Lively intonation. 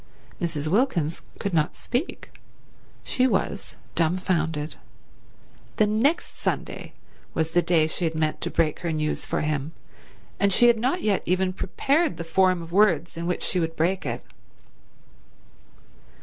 No: average, 4.2 semitones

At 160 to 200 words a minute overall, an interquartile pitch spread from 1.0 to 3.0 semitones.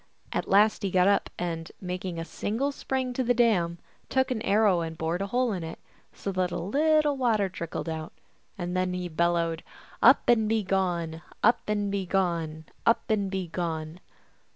No: average, 175 wpm; average, 4.4 semitones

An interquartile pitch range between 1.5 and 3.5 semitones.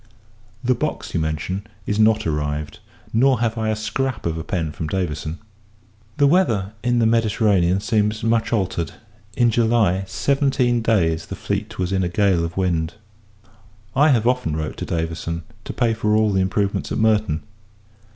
No: average, 5.3 semitones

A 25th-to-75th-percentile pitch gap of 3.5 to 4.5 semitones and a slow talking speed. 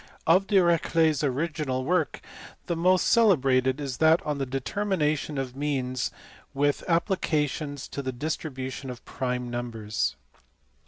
Yes: average, 4.2 semitones; slow, 130 wpm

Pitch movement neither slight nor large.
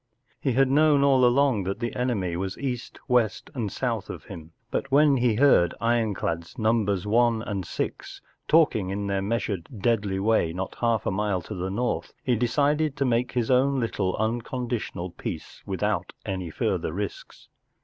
Yes: average, 4.5 semitones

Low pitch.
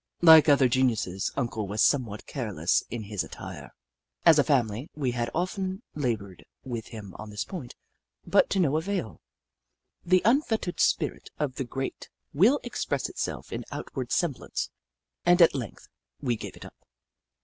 Yes: low, 130 Hz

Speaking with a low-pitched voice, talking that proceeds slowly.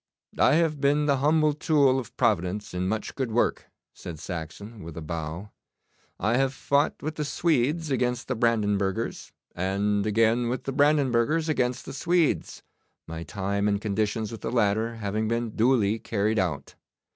No: low, 115 Hz; average, 160 wpm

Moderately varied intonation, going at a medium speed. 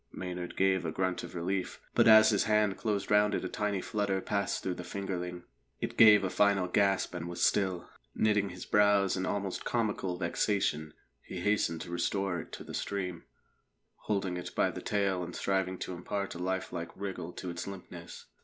No: narrow, 2.3 semitones; average, 190 wpm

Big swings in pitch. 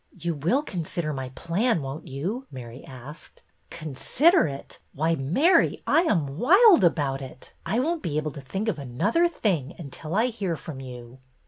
Yes: wide, 8.3 semitones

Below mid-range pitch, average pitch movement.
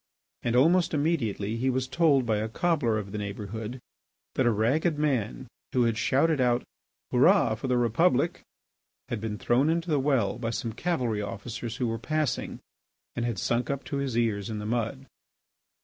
Yes: low, 120 Hz; average, 4.0 semitones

